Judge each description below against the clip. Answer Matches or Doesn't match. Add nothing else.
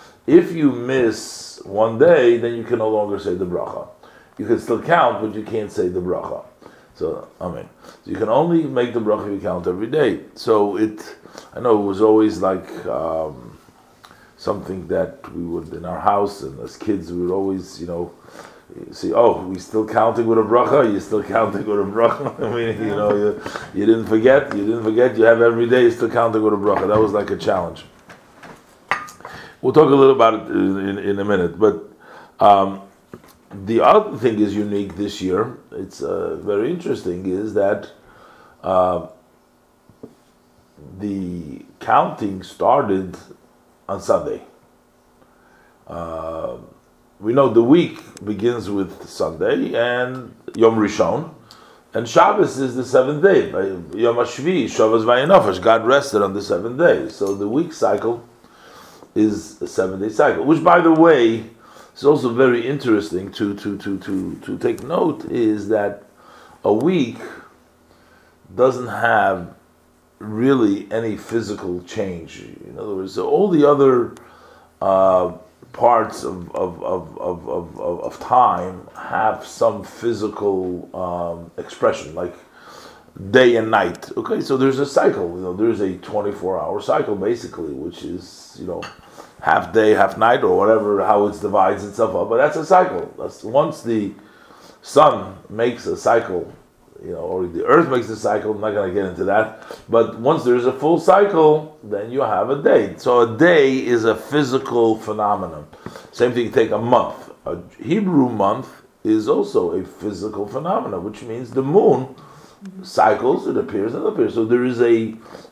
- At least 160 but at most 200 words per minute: Matches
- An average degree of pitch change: Matches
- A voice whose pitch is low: Matches